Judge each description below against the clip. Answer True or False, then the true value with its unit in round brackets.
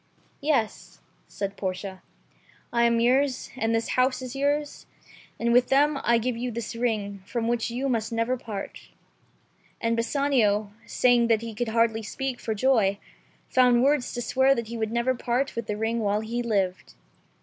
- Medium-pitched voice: False (235 Hz)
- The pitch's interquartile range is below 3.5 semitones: True (2.5 semitones)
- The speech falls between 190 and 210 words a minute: False (170 wpm)